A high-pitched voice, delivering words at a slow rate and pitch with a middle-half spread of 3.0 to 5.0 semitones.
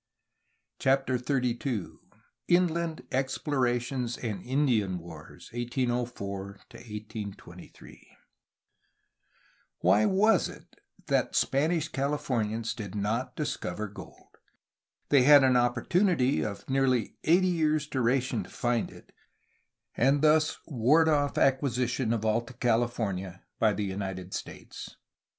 No: low, 125 Hz; slow, 105 wpm; average, 4.5 semitones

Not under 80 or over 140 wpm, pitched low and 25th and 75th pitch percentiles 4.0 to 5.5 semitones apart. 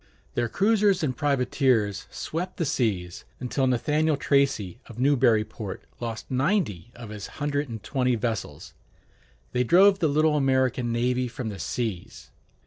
Yes: slow, 135 wpm; low, 125 Hz; average, 4.7 semitones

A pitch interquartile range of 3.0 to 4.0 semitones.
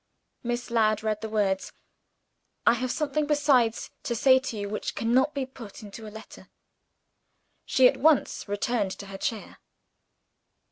Yes: average, 3.5 semitones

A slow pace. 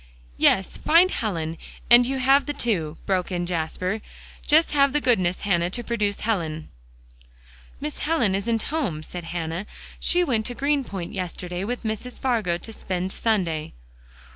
No: average, 150 wpm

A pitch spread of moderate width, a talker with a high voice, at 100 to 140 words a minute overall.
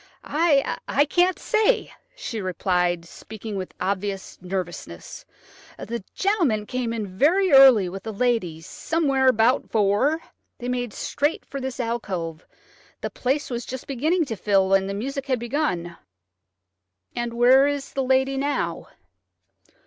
No: wide, 5.9 semitones; high, 240 Hz; slow, 135 wpm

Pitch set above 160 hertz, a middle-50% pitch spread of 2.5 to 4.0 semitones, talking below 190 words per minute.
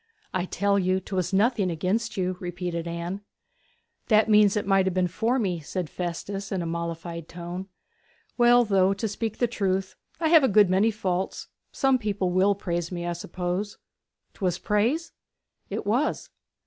Yes: high, 190 Hz; average, 3.1 semitones; average, 165 wpm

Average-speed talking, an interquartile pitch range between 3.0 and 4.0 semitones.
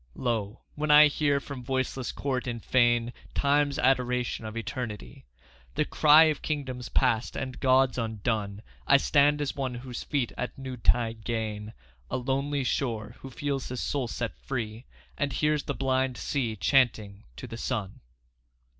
Yes: average, 155 wpm; average, 3.3 semitones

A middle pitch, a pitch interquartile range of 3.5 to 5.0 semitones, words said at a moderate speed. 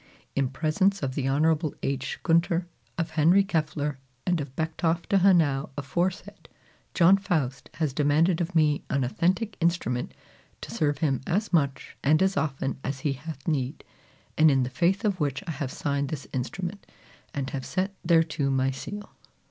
Yes: medium, 155 Hz; average, 4.1 semitones; average, 165 wpm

